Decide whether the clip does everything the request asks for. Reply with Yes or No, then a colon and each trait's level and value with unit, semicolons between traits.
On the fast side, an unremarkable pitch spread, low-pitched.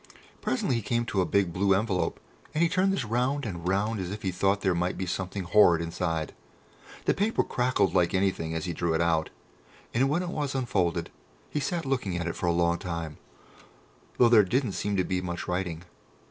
No: fast, 210 wpm; wide, 5.8 semitones; very low, 95 Hz